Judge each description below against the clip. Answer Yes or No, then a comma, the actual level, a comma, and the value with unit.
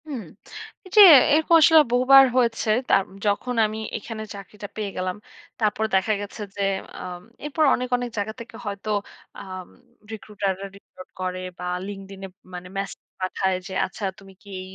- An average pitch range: Yes, average, 3.5 semitones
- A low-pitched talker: No, high, 205 Hz